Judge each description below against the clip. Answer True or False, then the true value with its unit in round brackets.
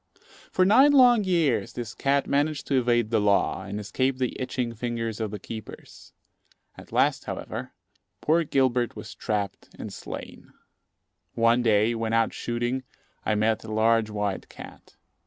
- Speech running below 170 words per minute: True (155 wpm)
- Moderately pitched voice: False (120 Hz)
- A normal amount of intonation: True (3.4 semitones)